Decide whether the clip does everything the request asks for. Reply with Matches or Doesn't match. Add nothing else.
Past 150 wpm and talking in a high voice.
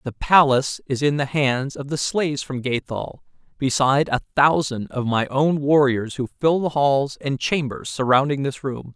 Doesn't match